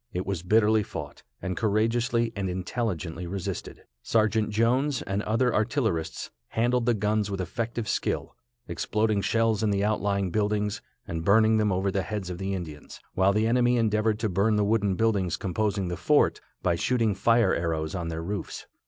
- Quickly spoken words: No, average, 170 wpm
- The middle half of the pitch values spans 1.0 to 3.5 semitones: Yes, average, 3.0 semitones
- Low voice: Yes, low, 105 Hz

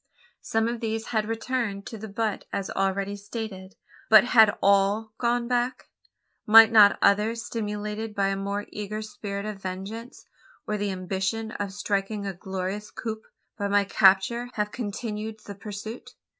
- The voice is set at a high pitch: Yes, high, 210 Hz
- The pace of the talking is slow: No, average, 155 wpm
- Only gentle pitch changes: Yes, narrow, 2.0 semitones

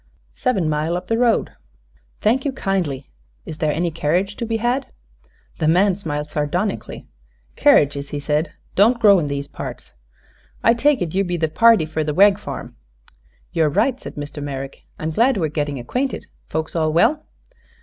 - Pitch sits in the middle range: Yes, medium, 170 Hz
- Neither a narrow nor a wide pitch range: No, wide, 6.6 semitones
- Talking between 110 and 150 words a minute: No, average, 175 wpm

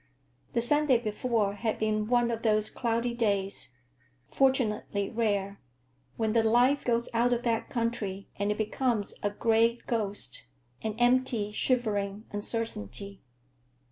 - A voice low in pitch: No, high, 220 Hz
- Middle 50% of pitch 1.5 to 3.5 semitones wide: Yes, average, 2.8 semitones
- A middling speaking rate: No, slow, 120 wpm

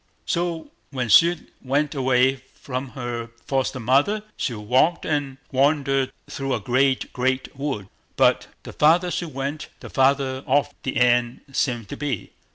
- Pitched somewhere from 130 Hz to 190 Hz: Yes, low, 135 Hz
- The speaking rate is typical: Yes, average, 150 wpm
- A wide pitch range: No, narrow, 2.4 semitones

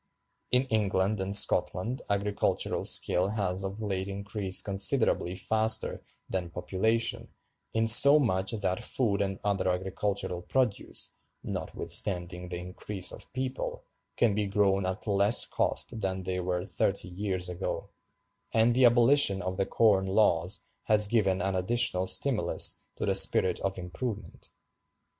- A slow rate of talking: Yes, slow, 130 wpm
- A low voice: Yes, low, 100 Hz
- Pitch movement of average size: Yes, average, 3.0 semitones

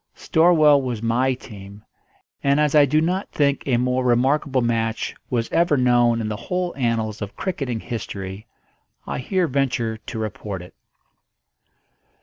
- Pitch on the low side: Yes, low, 125 Hz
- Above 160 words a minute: No, average, 145 wpm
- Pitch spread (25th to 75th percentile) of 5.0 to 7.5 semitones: No, average, 4.2 semitones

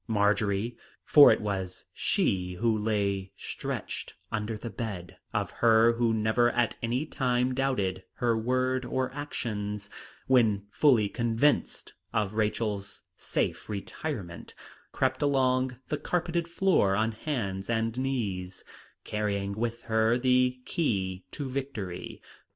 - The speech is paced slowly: Yes, slow, 120 wpm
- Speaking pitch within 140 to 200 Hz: No, low, 115 Hz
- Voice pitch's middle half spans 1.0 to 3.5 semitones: No, average, 3.9 semitones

